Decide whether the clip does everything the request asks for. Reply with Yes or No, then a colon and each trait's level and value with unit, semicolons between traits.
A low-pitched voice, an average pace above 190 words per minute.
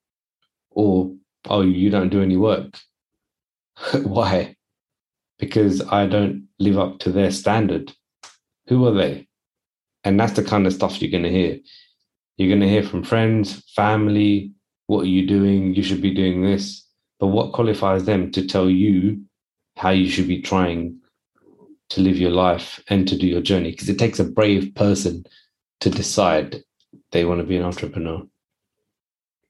No: very low, 95 Hz; average, 165 wpm